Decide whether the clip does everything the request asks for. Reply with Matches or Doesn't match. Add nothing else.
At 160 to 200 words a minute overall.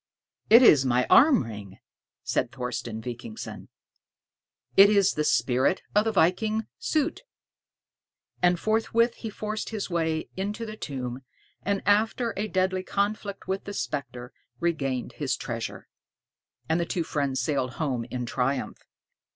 Doesn't match